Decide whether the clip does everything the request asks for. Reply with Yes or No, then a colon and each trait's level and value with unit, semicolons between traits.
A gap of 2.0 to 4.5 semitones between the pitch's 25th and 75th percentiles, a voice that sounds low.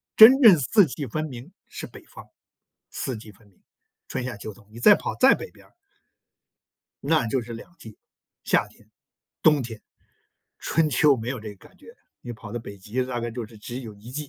No: average, 5.1 semitones; low, 120 Hz